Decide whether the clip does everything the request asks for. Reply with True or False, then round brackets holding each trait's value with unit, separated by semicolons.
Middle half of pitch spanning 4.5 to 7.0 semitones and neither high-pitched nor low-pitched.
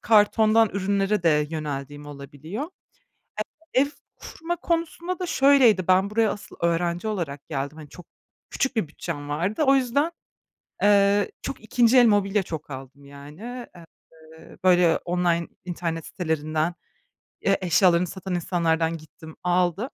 True (5.2 semitones; 180 Hz)